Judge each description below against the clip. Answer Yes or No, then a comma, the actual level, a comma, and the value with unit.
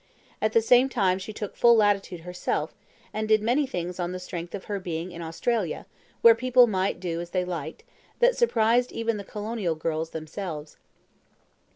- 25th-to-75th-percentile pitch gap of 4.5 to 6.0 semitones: Yes, average, 4.8 semitones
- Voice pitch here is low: No, high, 195 Hz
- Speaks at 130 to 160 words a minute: No, average, 180 wpm